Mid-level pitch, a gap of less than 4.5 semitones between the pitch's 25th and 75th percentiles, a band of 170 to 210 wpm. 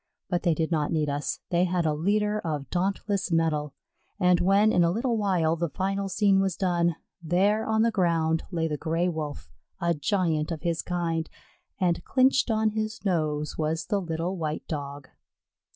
Yes: medium, 175 Hz; average, 3.6 semitones; average, 180 wpm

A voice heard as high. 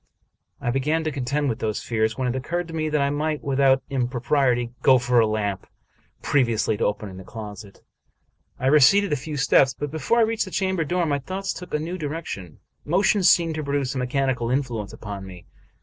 No: low, 135 Hz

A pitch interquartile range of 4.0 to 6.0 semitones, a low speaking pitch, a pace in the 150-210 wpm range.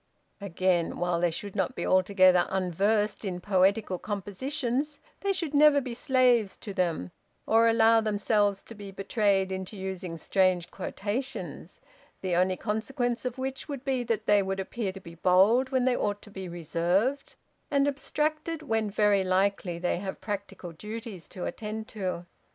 No: average, 4.3 semitones; high, 205 Hz; average, 160 wpm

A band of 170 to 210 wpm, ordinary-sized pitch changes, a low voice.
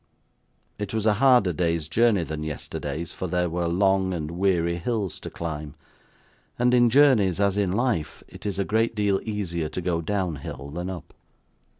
Yes: average, 180 wpm; average, 3.8 semitones; very low, 95 Hz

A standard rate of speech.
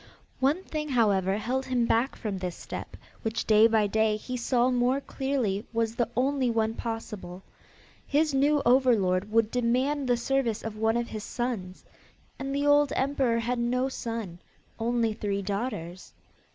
Yes: average, 160 wpm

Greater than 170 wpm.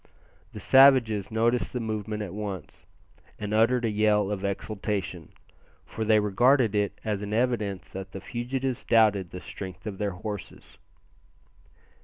No: average, 145 wpm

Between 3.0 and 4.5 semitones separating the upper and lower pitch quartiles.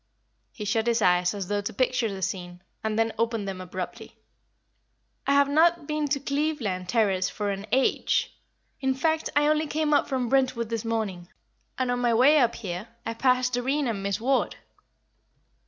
No: average, 5.3 semitones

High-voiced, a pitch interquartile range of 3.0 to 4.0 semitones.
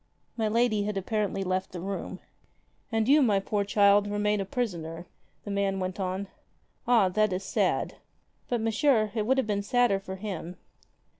No: high, 205 Hz; narrow, 2.4 semitones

